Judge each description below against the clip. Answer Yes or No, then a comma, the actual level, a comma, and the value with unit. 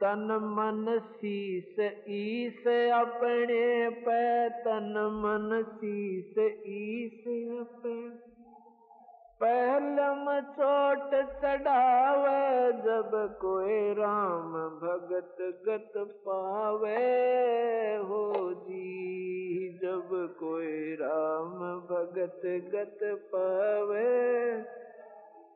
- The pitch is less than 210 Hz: No, high, 215 Hz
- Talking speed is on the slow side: Yes, slow, 65 wpm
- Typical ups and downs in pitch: Yes, average, 3.9 semitones